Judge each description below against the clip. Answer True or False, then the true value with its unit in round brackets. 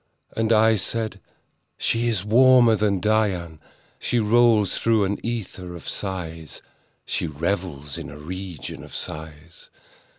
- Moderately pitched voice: False (100 Hz)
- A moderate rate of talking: False (125 wpm)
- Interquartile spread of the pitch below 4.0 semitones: False (4.9 semitones)